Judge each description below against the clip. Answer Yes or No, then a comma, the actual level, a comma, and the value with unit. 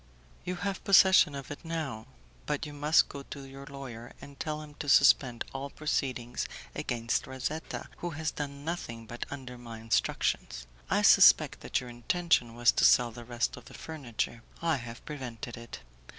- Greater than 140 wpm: Yes, average, 175 wpm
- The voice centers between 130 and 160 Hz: Yes, low, 135 Hz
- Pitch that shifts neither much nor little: Yes, average, 4.1 semitones